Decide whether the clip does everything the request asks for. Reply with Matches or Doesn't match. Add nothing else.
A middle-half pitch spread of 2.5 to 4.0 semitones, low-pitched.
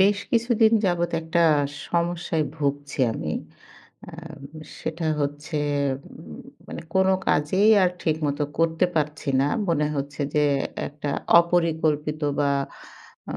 Doesn't match